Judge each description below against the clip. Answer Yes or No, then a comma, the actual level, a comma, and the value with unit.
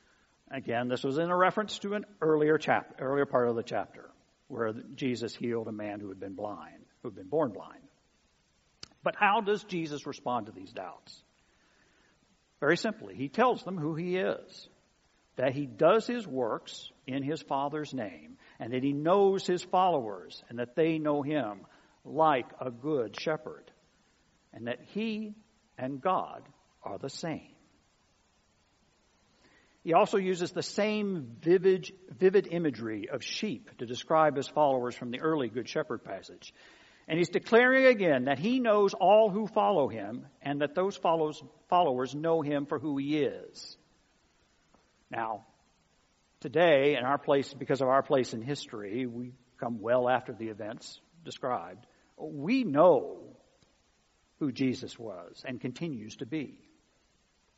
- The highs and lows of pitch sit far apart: Yes, wide, 6.4 semitones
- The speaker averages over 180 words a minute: No, average, 150 wpm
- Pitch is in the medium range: Yes, medium, 150 Hz